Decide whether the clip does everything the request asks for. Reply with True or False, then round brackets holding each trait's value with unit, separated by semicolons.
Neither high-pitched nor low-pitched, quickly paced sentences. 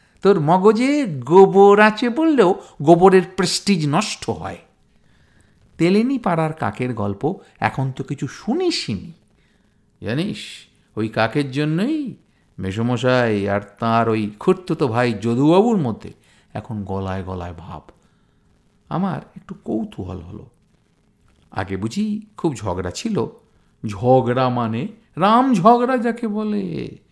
False (145 Hz; 110 wpm)